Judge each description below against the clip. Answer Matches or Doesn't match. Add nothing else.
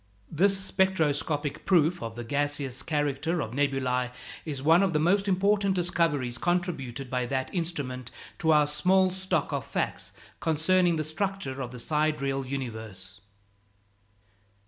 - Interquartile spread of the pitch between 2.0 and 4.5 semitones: Doesn't match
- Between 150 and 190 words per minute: Doesn't match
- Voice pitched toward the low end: Doesn't match